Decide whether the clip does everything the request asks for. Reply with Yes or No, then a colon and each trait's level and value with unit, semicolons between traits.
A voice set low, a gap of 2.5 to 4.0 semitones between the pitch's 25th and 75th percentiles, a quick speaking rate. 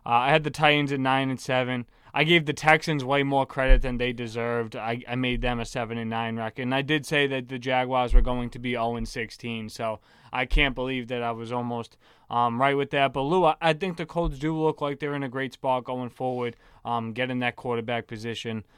Yes: low, 125 Hz; average, 2.9 semitones; fast, 245 wpm